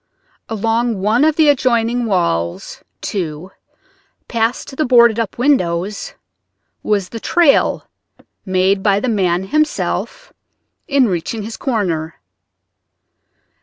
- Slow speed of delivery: Yes, slow, 105 wpm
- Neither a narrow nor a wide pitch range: Yes, average, 4.8 semitones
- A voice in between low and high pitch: No, high, 220 Hz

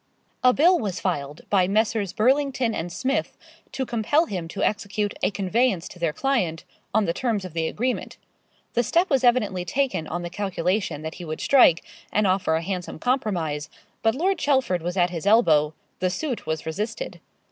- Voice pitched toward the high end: Yes, high, 200 Hz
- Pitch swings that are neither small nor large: No, wide, 6.5 semitones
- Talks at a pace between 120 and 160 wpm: No, average, 180 wpm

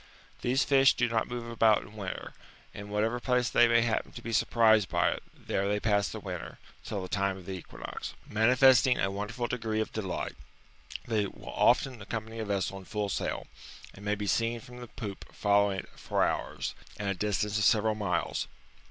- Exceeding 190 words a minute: Yes, fast, 205 wpm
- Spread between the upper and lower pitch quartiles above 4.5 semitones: No, narrow, 2.5 semitones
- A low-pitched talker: Yes, low, 110 Hz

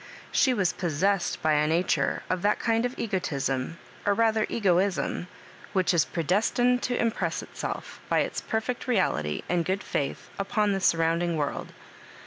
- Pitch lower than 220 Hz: Yes, medium, 185 Hz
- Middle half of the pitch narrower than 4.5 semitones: No, average, 5.0 semitones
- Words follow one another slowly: No, average, 155 wpm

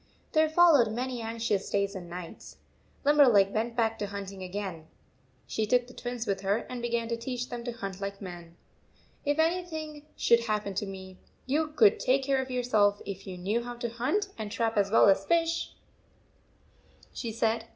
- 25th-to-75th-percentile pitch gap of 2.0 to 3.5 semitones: No, average, 4.2 semitones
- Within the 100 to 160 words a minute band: No, average, 180 wpm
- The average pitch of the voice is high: Yes, high, 230 Hz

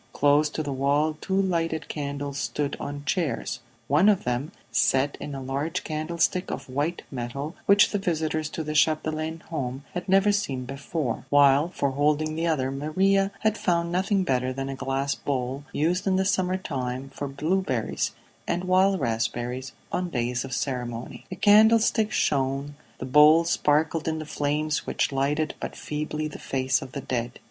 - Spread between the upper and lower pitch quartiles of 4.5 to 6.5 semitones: No, average, 4.0 semitones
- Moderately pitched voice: Yes, medium, 150 Hz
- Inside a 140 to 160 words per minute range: No, average, 170 wpm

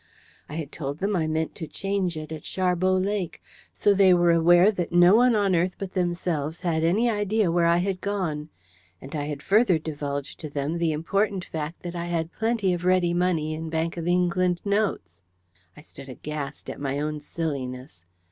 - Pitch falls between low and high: Yes, medium, 170 Hz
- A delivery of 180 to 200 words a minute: Yes, average, 195 wpm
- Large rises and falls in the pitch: No, average, 3.4 semitones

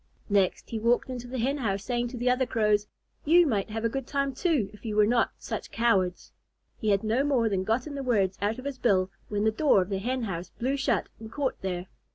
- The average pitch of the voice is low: No, high, 230 Hz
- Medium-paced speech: No, fast, 240 wpm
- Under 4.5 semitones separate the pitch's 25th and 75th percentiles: Yes, average, 4.1 semitones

